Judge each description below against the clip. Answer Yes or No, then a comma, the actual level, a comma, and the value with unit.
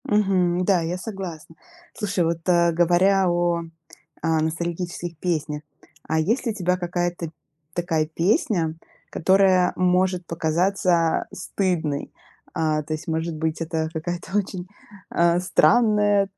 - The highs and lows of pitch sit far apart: No, narrow, 2.4 semitones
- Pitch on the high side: No, medium, 175 Hz